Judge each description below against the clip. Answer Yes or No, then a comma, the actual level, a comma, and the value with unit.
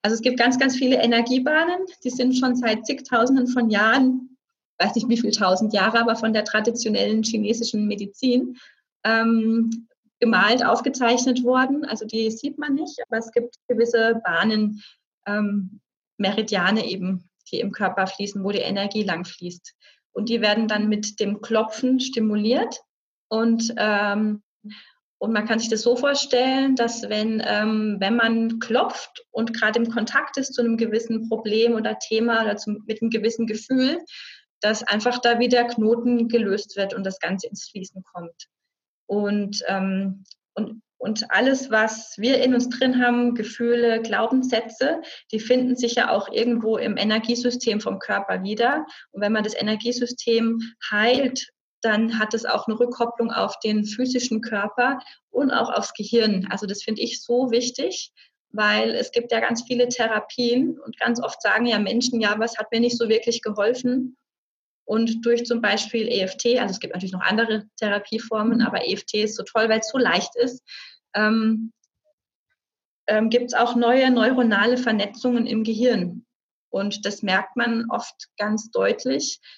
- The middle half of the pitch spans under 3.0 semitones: Yes, narrow, 2.4 semitones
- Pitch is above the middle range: Yes, high, 230 Hz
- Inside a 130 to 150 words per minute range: No, average, 160 wpm